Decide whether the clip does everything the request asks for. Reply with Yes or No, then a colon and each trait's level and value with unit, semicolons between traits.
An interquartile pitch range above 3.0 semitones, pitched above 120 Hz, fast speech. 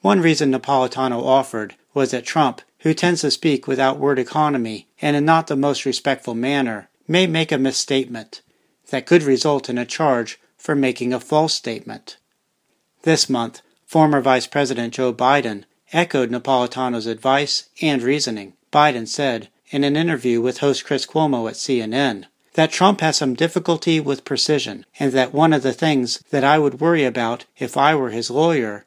No: average, 3.5 semitones; low, 135 Hz; average, 170 wpm